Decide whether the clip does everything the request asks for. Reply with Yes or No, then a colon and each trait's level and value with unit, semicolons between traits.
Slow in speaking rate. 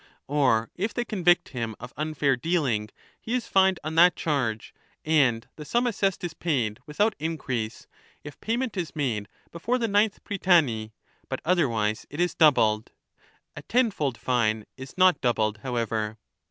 No: average, 160 wpm